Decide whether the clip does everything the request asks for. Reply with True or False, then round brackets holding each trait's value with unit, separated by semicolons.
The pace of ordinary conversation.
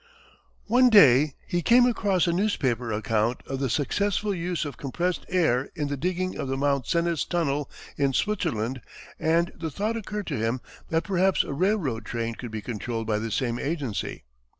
True (175 wpm)